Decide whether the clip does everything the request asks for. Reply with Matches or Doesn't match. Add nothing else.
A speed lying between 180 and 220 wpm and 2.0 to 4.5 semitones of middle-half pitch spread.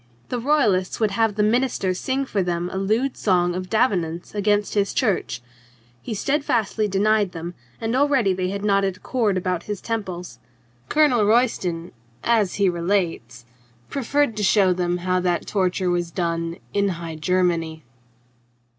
Doesn't match